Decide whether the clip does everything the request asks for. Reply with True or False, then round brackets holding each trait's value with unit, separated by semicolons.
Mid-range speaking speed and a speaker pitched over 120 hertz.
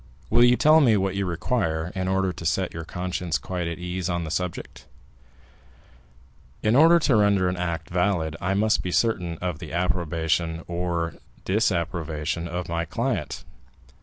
False (165 wpm; 90 Hz)